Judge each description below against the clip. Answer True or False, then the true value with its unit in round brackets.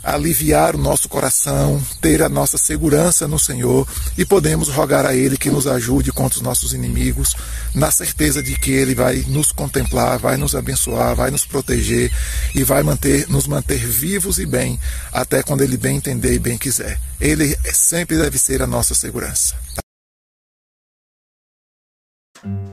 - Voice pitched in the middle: False (130 Hz)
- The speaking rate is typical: True (155 wpm)